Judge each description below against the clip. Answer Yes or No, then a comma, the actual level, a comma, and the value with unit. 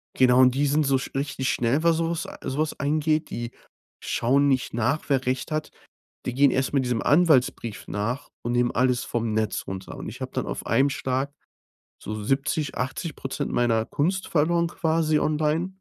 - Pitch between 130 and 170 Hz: Yes, low, 135 Hz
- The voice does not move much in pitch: No, average, 3.8 semitones